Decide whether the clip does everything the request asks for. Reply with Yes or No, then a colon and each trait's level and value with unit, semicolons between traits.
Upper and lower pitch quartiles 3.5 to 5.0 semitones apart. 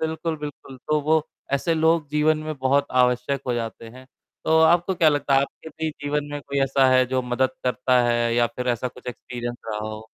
Yes: average, 3.8 semitones